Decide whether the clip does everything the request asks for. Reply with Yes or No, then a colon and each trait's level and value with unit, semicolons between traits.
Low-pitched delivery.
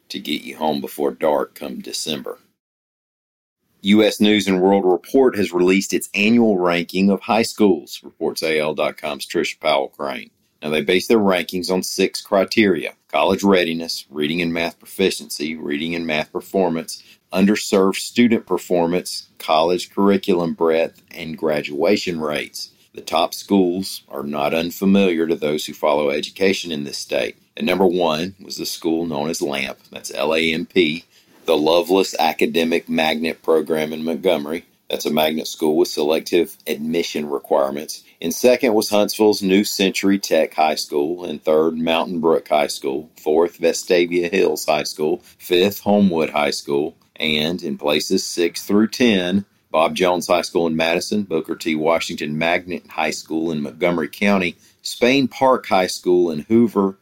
Yes: very low, 90 Hz